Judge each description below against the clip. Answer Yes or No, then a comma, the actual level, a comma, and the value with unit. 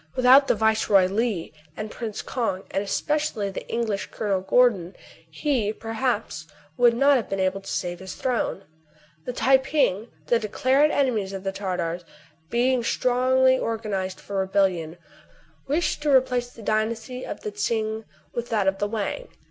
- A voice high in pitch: Yes, high, 220 Hz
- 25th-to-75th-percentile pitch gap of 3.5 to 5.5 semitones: Yes, average, 4.3 semitones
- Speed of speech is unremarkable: Yes, average, 165 wpm